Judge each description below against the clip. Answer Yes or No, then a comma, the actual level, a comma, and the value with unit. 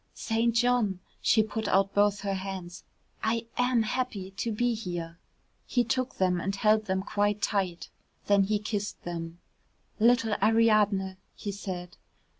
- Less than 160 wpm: Yes, average, 145 wpm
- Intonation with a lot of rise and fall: No, average, 2.8 semitones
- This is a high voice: Yes, high, 205 Hz